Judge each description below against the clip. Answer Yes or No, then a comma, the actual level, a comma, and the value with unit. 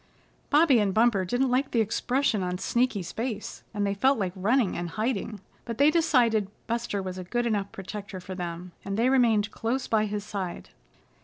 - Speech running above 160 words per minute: Yes, average, 185 wpm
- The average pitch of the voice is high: Yes, high, 215 Hz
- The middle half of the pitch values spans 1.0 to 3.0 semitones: No, average, 4.0 semitones